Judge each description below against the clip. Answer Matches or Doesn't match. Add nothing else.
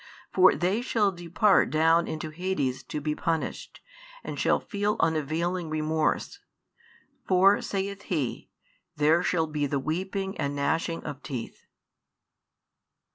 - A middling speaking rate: Doesn't match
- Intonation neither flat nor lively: Matches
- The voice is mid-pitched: Matches